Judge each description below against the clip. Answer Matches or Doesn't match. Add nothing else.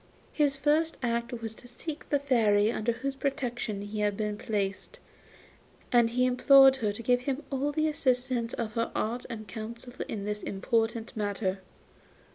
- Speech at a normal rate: Matches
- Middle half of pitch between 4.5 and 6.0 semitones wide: Doesn't match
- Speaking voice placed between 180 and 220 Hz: Doesn't match